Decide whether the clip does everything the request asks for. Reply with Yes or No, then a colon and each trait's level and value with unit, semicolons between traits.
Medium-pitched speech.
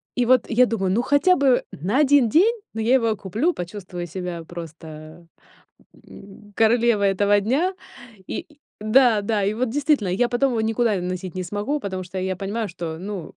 No: high, 210 Hz